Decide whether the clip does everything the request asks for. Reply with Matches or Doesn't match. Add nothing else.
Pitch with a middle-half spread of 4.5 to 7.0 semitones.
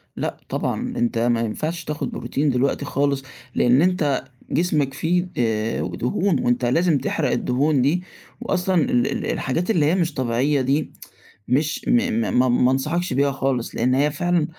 Matches